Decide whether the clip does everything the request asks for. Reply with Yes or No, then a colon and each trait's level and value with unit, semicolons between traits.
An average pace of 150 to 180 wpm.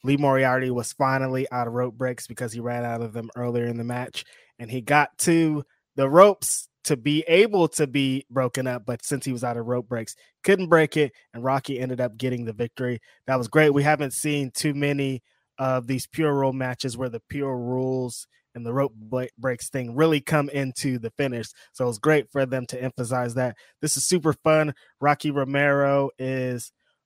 No: fast, 205 wpm